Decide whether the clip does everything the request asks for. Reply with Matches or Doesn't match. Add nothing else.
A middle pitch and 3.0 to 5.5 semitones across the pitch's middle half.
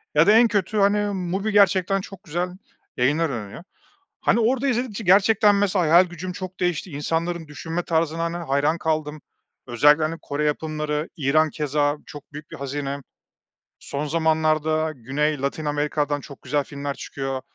Matches